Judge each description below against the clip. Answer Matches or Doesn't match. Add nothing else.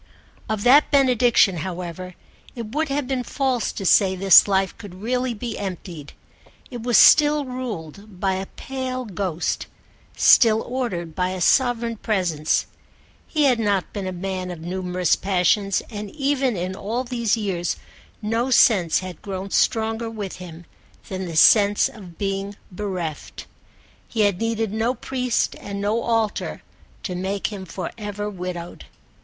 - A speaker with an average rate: Matches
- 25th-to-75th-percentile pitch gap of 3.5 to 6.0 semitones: Matches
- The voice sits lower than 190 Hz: Doesn't match